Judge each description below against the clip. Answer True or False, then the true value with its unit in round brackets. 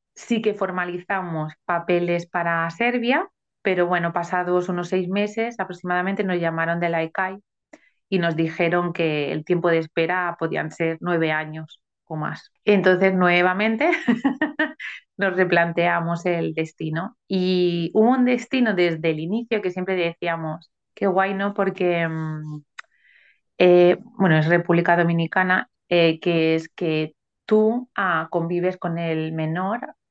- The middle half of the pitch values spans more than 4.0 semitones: False (2.7 semitones)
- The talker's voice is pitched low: False (175 Hz)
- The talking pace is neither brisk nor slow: True (135 wpm)